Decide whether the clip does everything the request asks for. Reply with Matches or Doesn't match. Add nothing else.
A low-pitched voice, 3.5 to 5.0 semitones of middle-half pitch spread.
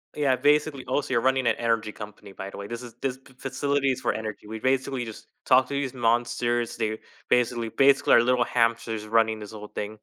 Doesn't match